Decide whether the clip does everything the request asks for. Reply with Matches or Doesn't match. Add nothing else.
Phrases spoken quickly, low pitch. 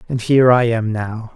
Matches